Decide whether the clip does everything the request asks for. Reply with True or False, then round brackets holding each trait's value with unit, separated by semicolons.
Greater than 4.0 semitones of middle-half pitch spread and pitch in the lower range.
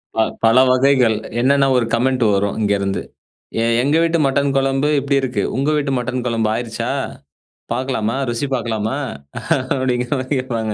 False (3.0 semitones; 125 Hz)